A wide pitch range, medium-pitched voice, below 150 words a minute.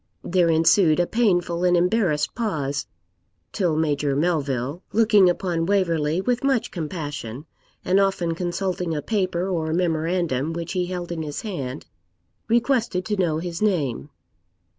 No: average, 3.4 semitones; medium, 175 Hz; average, 140 wpm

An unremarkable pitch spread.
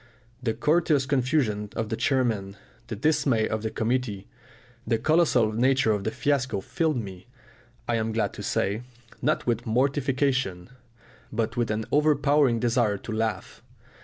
Yes: average, 4.0 semitones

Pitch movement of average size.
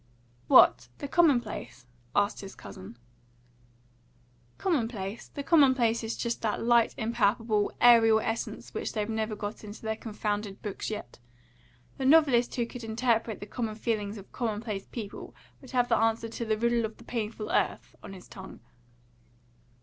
No: narrow, 2.2 semitones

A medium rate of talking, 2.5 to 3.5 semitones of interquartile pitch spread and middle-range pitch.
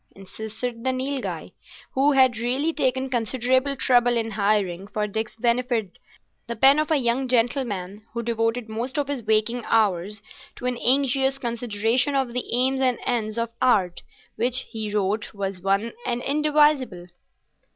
No: average, 150 wpm; average, 3.2 semitones; high, 240 Hz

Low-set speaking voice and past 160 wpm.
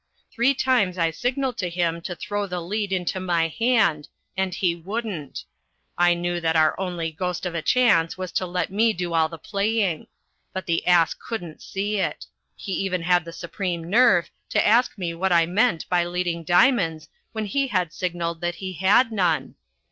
No: medium, 180 Hz; average, 185 wpm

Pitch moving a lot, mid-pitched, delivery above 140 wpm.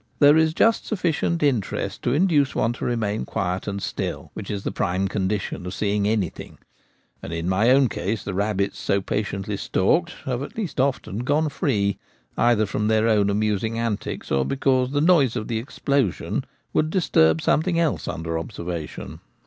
No: wide, 6.1 semitones; low, 110 Hz; average, 175 wpm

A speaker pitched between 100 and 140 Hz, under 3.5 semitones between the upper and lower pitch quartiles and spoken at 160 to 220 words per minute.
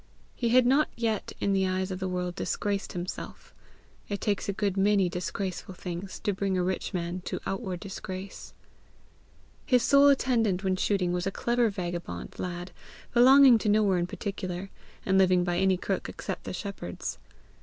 No: high, 190 Hz; narrow, 2.5 semitones; average, 170 wpm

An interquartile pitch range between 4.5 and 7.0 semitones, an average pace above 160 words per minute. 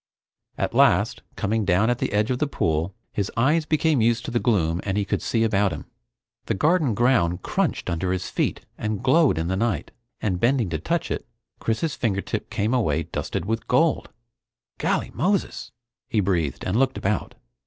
Yes: wide, 5.4 semitones; average, 185 wpm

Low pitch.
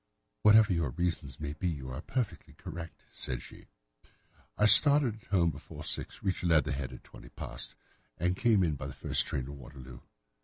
Yes: very low, 80 Hz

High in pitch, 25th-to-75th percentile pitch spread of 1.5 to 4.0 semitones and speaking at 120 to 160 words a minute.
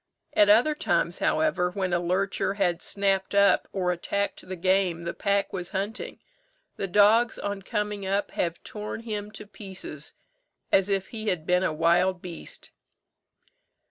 Yes: high, 195 Hz; narrow, 2.4 semitones; average, 155 wpm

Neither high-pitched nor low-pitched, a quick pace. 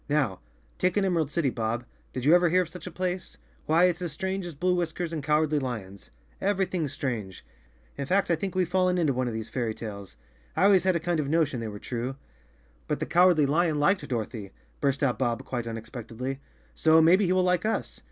Yes: medium, 155 Hz; fast, 215 wpm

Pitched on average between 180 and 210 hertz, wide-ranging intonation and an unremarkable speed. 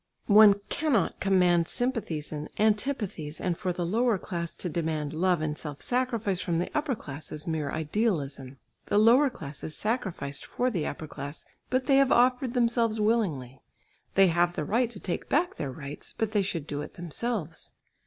Yes: medium, 185 Hz; wide, 6.9 semitones; average, 180 wpm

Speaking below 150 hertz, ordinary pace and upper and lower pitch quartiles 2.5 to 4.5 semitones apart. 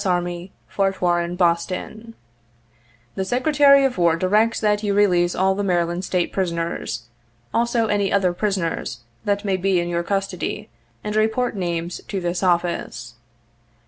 No: medium, 185 Hz; average, 150 wpm; average, 3.1 semitones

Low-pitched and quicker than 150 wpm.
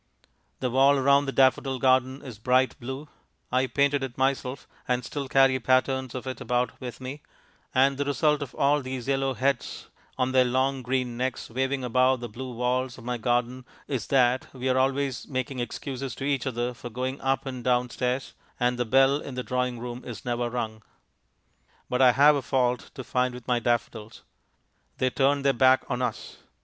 Yes: low, 130 Hz; average, 190 wpm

